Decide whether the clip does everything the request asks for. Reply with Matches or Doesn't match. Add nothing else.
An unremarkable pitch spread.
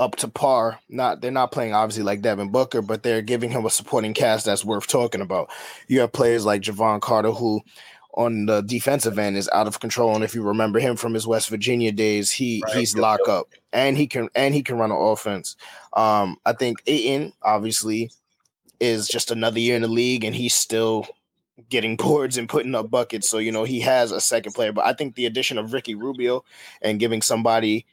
Doesn't match